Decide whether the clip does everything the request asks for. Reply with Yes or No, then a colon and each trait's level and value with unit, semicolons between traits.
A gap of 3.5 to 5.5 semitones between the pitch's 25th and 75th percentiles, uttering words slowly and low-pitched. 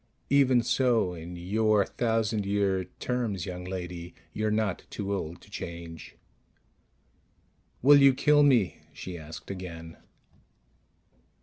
Yes: average, 4.7 semitones; slow, 115 wpm; low, 100 Hz